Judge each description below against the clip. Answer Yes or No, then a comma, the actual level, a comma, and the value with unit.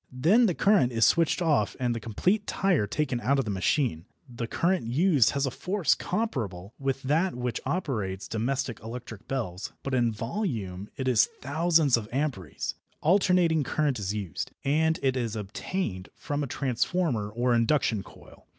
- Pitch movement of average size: No, wide, 6.2 semitones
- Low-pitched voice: Yes, low, 130 Hz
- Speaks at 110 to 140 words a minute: No, average, 165 wpm